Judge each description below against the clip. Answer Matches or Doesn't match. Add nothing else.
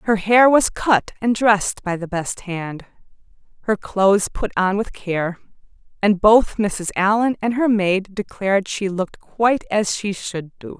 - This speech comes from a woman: Matches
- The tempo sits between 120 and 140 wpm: Doesn't match